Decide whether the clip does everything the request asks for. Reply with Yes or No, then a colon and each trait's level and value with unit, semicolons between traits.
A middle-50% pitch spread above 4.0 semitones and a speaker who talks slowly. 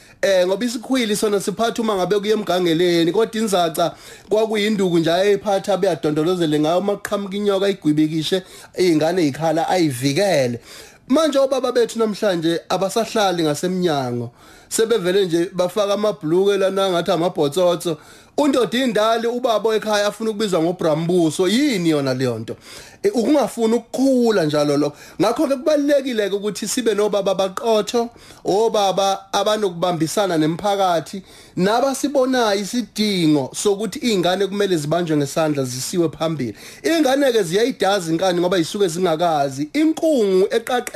Yes: average, 4.8 semitones; slow, 115 wpm